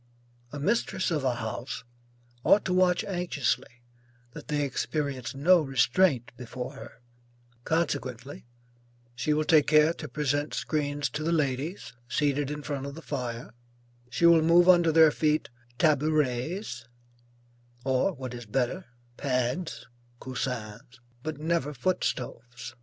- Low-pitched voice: No, medium, 145 Hz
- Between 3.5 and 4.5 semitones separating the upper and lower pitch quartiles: Yes, average, 4.2 semitones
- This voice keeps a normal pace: No, slow, 130 wpm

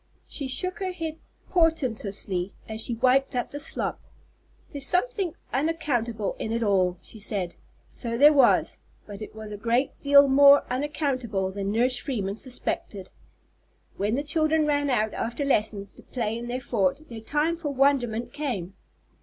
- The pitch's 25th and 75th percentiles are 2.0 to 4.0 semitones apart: No, average, 5.1 semitones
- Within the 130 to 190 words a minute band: Yes, average, 160 wpm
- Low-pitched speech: No, very high, 250 Hz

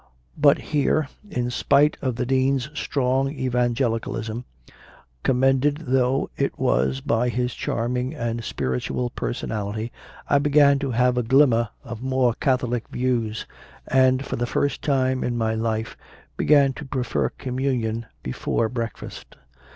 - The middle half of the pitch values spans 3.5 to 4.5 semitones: No, narrow, 2.6 semitones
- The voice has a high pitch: No, low, 125 Hz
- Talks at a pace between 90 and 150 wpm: Yes, average, 140 wpm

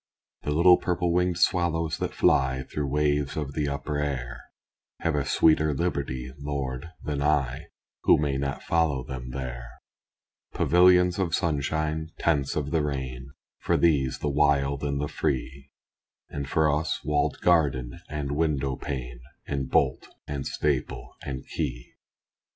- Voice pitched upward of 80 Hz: No, very low, 70 Hz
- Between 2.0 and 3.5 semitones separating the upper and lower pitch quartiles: Yes, narrow, 2.6 semitones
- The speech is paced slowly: No, average, 145 wpm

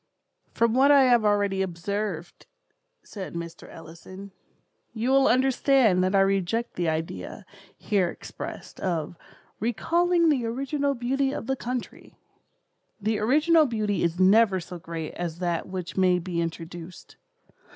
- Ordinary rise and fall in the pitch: No, wide, 6.3 semitones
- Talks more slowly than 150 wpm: Yes, slow, 135 wpm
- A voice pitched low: No, high, 200 Hz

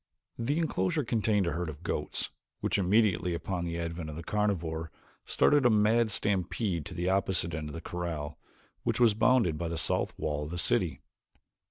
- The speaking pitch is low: Yes, very low, 90 Hz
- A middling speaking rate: Yes, average, 185 wpm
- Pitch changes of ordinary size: Yes, average, 4.5 semitones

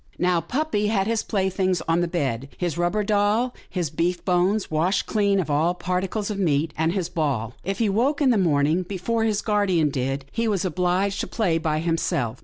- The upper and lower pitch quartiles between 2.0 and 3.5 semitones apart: No, average, 4.0 semitones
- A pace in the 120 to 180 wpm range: No, fast, 205 wpm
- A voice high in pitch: No, medium, 180 Hz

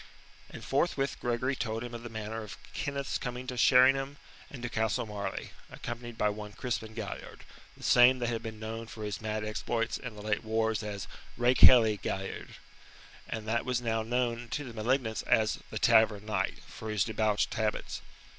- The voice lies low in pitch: Yes, low, 115 Hz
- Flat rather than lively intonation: Yes, narrow, 2.2 semitones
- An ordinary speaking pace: Yes, average, 180 wpm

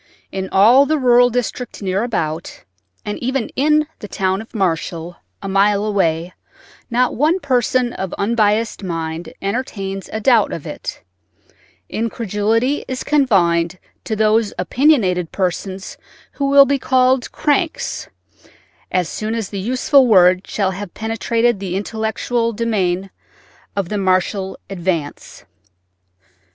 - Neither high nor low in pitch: No, high, 210 Hz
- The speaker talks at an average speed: No, slow, 125 wpm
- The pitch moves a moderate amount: Yes, average, 4.6 semitones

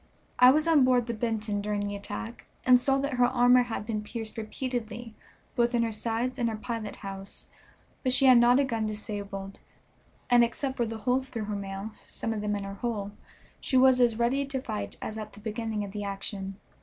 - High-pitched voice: Yes, high, 225 Hz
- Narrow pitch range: No, average, 3.0 semitones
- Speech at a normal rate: No, fast, 215 wpm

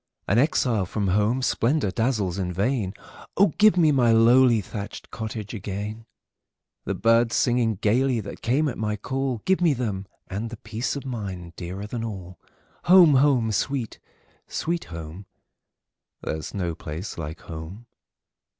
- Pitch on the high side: No, low, 110 Hz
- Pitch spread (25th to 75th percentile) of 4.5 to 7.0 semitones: Yes, average, 4.9 semitones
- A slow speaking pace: Yes, slow, 130 wpm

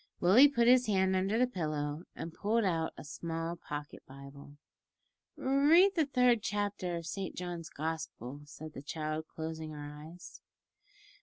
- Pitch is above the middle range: No, medium, 170 Hz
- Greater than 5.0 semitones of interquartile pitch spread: Yes, wide, 5.5 semitones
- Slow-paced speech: No, average, 150 wpm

